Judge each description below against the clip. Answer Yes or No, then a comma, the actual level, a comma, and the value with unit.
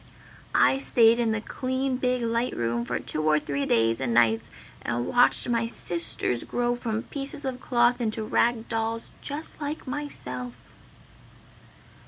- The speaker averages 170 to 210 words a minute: No, average, 150 wpm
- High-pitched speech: Yes, high, 230 Hz